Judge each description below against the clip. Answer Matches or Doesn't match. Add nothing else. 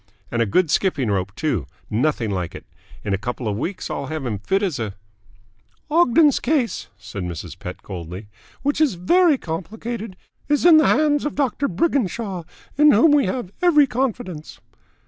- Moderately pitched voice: Matches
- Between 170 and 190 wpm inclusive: Matches